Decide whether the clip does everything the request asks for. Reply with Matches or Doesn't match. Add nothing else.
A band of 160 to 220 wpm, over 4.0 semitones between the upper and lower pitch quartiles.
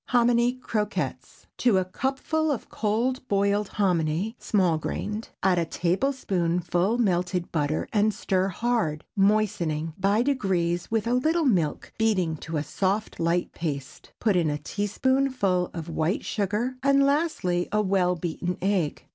Doesn't match